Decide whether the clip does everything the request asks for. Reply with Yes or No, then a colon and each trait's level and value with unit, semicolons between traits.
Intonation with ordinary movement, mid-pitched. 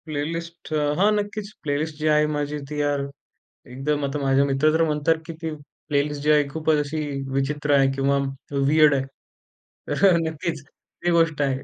No: narrow, 2.1 semitones; medium, 150 Hz